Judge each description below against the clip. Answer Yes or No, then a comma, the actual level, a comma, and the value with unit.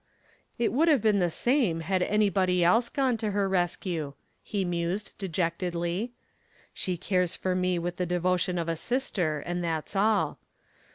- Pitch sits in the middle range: Yes, medium, 180 Hz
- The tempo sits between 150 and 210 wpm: Yes, average, 160 wpm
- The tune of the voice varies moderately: Yes, average, 3.2 semitones